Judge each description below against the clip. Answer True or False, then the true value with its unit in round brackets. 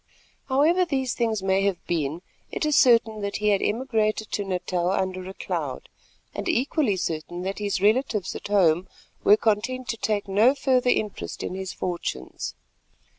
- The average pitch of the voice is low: False (210 Hz)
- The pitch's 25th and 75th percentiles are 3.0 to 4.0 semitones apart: False (4.7 semitones)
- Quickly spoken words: False (165 wpm)